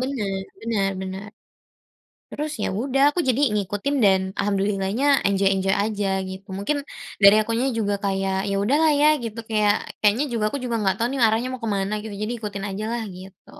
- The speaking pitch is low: No, high, 210 Hz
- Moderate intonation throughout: Yes, average, 3.1 semitones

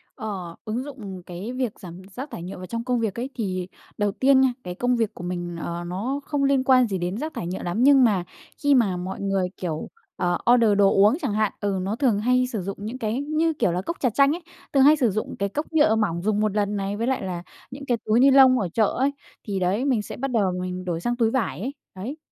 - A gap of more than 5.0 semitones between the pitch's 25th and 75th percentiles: Yes, wide, 5.5 semitones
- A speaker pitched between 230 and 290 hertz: No, high, 215 Hz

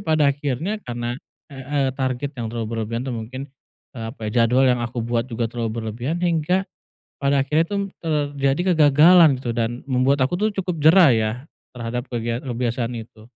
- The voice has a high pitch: No, low, 130 Hz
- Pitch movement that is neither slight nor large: Yes, average, 4.2 semitones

